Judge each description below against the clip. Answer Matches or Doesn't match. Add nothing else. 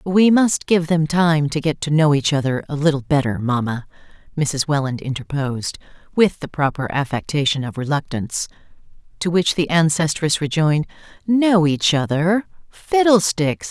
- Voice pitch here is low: Doesn't match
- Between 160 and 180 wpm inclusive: Doesn't match